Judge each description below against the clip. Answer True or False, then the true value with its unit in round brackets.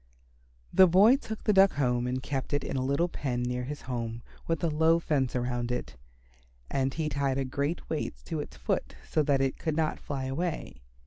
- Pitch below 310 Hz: True (140 Hz)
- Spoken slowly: False (205 wpm)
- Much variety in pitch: False (4.0 semitones)